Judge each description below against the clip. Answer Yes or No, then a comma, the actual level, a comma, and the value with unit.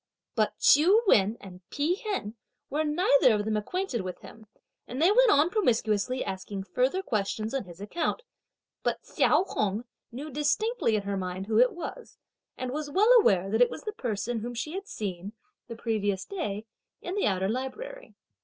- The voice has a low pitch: No, high, 240 Hz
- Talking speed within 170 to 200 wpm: Yes, average, 180 wpm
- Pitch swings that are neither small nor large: No, wide, 8.3 semitones